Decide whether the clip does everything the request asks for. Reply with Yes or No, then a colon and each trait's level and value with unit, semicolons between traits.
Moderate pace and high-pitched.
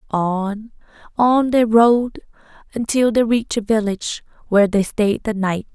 Yes: average, 145 wpm; high, 220 Hz